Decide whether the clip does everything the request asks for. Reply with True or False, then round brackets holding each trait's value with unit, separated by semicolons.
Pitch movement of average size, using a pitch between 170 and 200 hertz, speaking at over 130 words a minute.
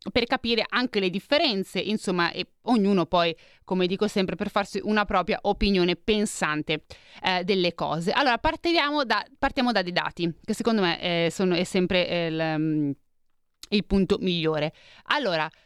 True (3.7 semitones; 190 Hz; 155 wpm)